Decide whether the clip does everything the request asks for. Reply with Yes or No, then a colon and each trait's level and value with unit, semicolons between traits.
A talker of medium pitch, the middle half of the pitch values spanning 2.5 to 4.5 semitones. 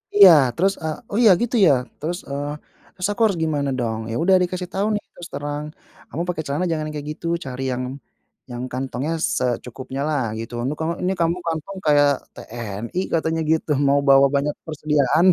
Yes: medium, 150 Hz; average, 4.1 semitones